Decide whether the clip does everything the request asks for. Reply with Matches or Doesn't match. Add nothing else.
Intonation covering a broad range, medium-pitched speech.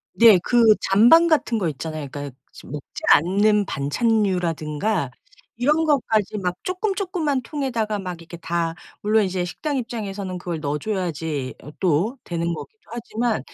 Doesn't match